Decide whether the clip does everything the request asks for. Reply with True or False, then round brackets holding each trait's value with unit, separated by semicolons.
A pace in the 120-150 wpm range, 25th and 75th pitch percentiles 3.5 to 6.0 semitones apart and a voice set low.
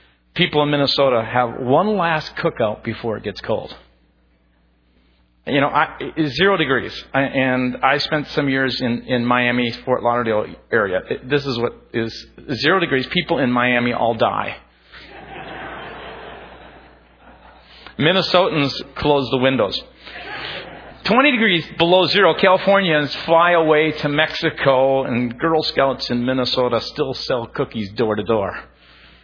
True (135 wpm; 5.2 semitones; 130 Hz)